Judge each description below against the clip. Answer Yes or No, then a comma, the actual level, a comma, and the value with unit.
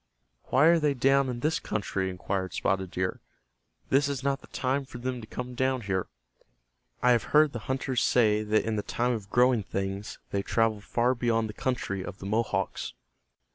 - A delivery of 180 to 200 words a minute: Yes, average, 190 wpm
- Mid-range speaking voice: No, low, 120 Hz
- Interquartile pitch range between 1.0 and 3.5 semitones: No, average, 4.2 semitones